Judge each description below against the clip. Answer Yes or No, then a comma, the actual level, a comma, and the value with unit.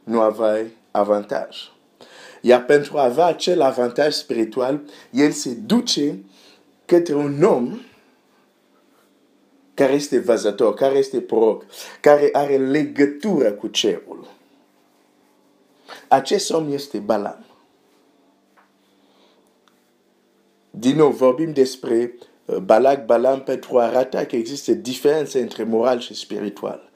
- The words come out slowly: Yes, slow, 105 wpm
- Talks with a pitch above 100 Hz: Yes, medium, 140 Hz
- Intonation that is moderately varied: Yes, average, 4.1 semitones